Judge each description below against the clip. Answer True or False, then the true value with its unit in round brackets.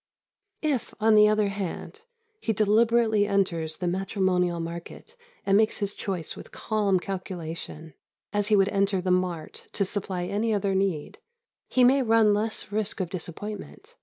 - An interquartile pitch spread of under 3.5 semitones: True (2.9 semitones)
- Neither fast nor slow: True (155 wpm)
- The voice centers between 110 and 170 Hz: False (200 Hz)